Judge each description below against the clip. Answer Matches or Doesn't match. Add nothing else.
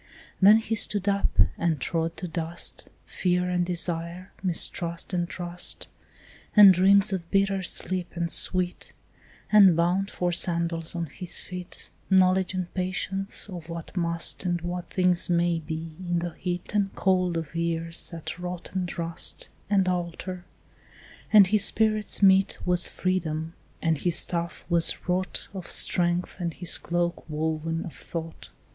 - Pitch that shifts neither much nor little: Doesn't match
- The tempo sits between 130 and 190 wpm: Matches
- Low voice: Doesn't match